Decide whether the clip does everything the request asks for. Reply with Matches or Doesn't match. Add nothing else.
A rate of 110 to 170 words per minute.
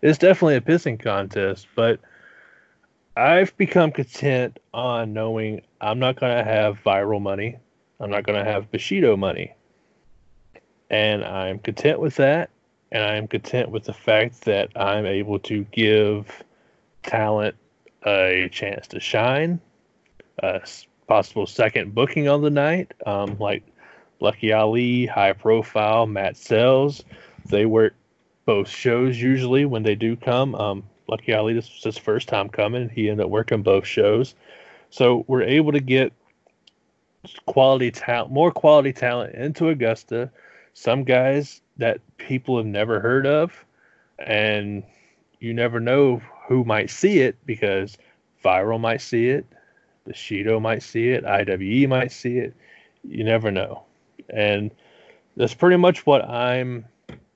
Matches